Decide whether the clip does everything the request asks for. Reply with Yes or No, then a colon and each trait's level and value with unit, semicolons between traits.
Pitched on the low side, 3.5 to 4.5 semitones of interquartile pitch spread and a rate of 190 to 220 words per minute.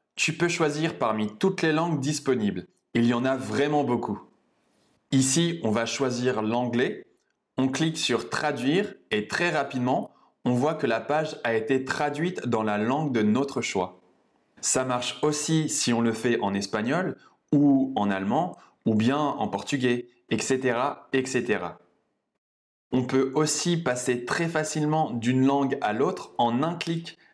No: low, 130 Hz; average, 4.2 semitones; average, 155 wpm